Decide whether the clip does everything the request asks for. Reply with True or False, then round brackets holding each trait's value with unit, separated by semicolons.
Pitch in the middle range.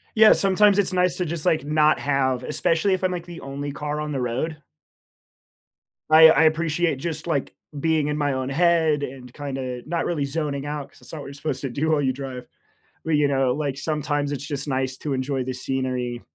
True (145 Hz)